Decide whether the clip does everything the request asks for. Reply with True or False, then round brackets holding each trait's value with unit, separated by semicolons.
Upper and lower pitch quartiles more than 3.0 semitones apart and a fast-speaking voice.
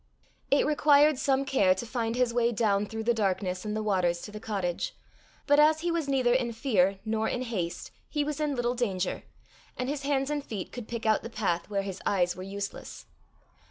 True (5.4 semitones; 210 wpm)